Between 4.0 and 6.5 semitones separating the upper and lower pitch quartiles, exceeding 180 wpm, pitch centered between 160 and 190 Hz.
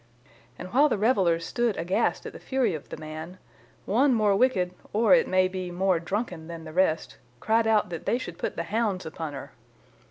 Yes: average, 5.0 semitones; average, 200 wpm; medium, 185 Hz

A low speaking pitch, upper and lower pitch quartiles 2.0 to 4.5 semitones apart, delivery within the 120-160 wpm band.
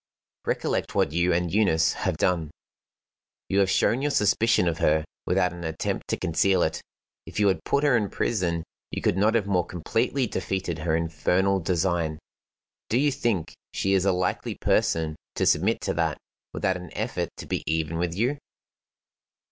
No: very low, 90 Hz; average, 3.7 semitones; average, 175 wpm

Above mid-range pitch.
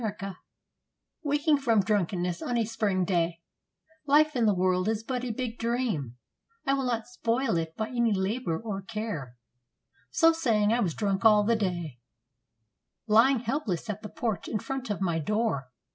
Yes: high, 220 Hz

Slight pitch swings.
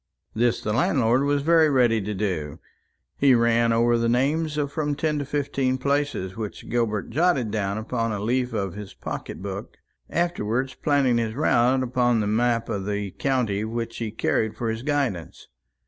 No: average, 4.1 semitones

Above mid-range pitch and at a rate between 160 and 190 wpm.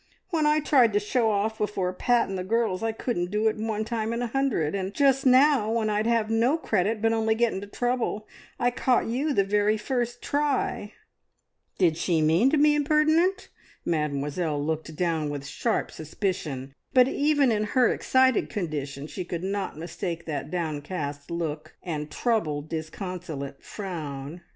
Yes: high, 210 Hz; average, 170 wpm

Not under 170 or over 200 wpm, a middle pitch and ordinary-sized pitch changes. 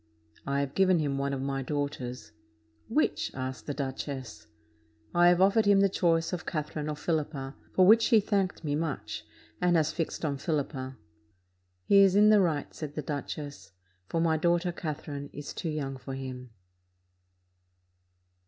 No: average, 160 wpm; medium, 150 Hz; average, 4.2 semitones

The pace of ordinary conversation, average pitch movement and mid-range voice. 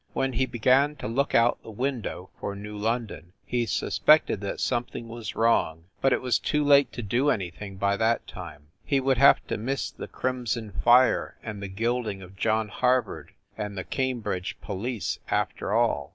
No: average, 180 wpm; average, 4.2 semitones; low, 115 Hz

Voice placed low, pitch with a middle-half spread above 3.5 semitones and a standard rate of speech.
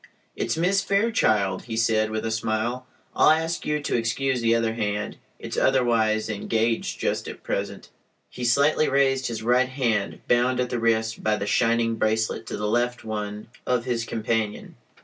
No: low, 115 Hz; narrow, 2.6 semitones; average, 170 wpm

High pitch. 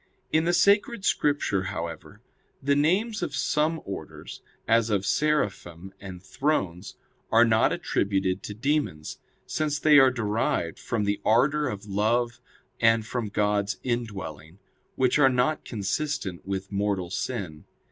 No: low, 110 Hz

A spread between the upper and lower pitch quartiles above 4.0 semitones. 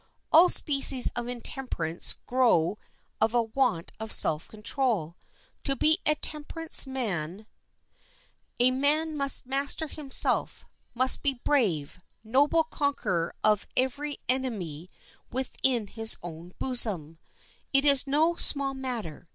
Yes: wide, 5.5 semitones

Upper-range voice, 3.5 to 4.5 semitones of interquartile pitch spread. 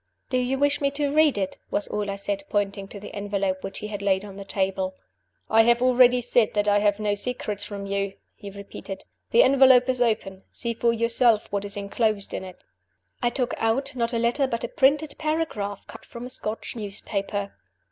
Yes: high, 215 Hz; average, 3.8 semitones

